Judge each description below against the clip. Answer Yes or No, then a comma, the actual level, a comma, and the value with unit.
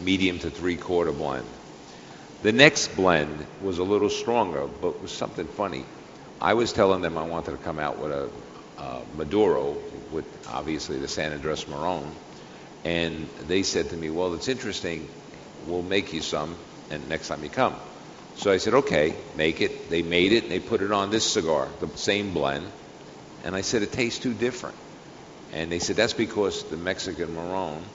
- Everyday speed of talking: Yes, average, 185 wpm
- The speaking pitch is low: Yes, very low, 90 Hz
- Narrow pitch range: No, average, 3.4 semitones